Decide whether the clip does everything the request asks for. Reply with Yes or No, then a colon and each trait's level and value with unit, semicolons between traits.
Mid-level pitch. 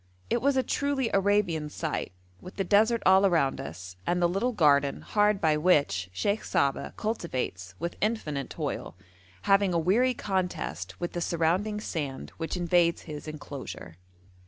Yes: medium, 175 Hz